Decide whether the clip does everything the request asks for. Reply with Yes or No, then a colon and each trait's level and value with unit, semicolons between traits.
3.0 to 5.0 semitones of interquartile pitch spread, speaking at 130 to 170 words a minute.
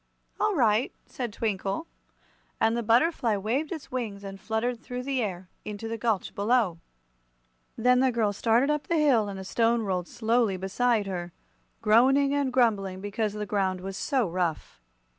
Yes: average, 4.0 semitones; average, 165 wpm